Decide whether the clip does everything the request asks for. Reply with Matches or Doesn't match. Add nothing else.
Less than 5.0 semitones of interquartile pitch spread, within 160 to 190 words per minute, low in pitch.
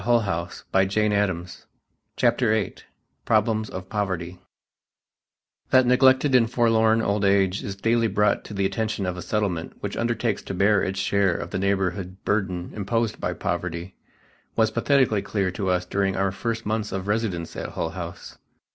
Matches